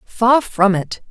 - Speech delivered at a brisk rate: No, average, 165 wpm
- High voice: Yes, high, 210 Hz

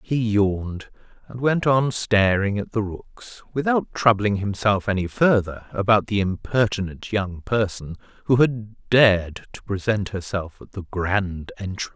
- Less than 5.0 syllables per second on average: Yes, 4.3 syllables/s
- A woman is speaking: No, male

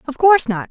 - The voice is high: Yes, very high, 290 Hz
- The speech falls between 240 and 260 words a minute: Yes, fast, 255 wpm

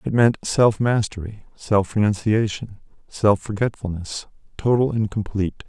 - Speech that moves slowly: Yes, slow, 115 wpm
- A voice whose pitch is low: Yes, low, 105 Hz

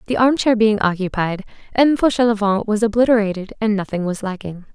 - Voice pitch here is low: No, high, 210 Hz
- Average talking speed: Yes, average, 165 wpm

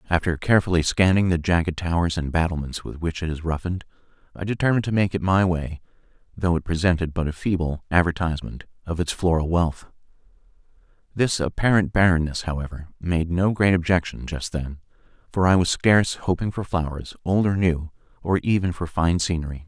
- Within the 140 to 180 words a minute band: Yes, average, 170 wpm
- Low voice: Yes, very low, 85 Hz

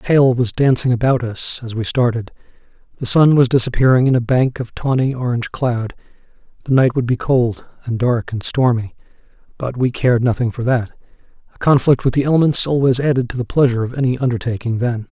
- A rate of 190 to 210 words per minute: Yes, average, 195 wpm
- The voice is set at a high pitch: No, low, 125 Hz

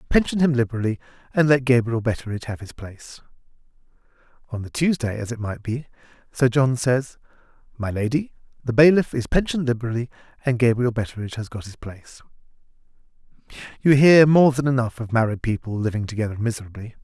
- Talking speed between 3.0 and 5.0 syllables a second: No, 6.3 syllables/s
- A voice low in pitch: Yes, low, 120 Hz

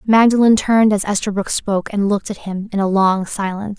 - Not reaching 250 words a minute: Yes, fast, 205 wpm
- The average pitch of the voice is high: Yes, high, 205 Hz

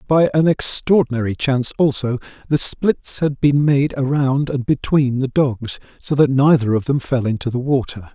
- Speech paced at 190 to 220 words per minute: No, average, 175 wpm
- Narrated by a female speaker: No, male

